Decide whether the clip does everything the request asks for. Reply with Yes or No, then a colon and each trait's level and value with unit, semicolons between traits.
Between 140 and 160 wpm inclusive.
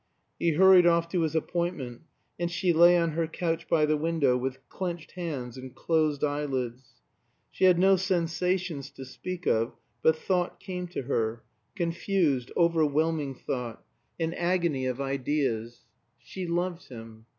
Yes: average, 150 wpm